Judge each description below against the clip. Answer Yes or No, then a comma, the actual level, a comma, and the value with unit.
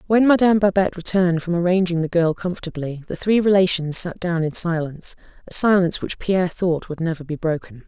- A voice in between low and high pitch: Yes, medium, 175 Hz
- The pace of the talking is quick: No, average, 190 wpm